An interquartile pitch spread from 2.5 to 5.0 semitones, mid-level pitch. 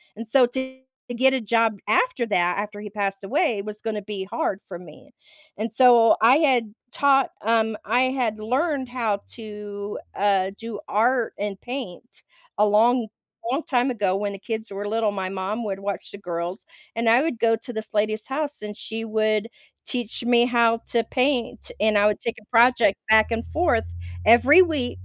No: average, 3.1 semitones; high, 225 Hz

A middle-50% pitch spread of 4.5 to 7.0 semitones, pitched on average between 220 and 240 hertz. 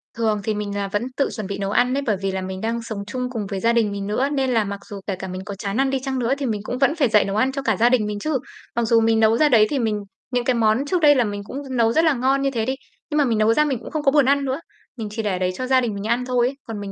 No: average, 4.1 semitones; high, 230 Hz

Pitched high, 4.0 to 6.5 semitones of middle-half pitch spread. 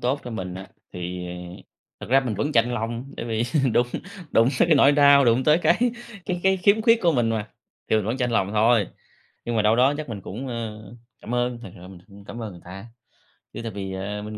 No: low, 115 Hz; average, 4.7 semitones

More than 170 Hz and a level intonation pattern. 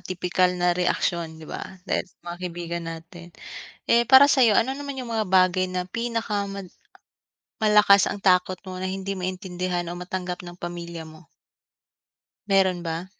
Yes: medium, 185 Hz; narrow, 2.2 semitones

